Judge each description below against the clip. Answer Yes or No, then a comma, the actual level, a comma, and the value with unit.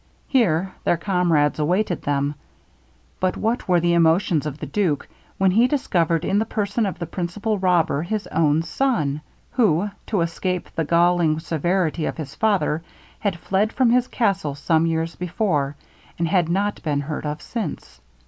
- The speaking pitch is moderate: Yes, medium, 175 Hz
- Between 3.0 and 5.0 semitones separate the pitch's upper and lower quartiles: Yes, average, 4.2 semitones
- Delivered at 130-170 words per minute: Yes, average, 165 wpm